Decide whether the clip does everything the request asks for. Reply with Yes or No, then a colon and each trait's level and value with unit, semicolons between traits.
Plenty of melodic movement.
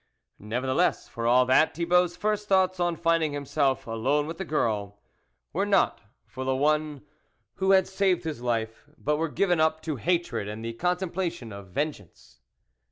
Yes: wide, 6.3 semitones